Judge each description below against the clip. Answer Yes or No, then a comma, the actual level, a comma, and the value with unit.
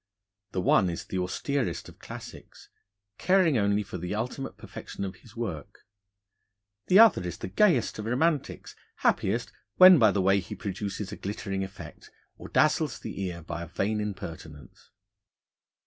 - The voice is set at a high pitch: No, low, 100 Hz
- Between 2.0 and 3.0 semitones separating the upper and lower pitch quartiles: No, average, 4.5 semitones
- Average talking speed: Yes, average, 155 wpm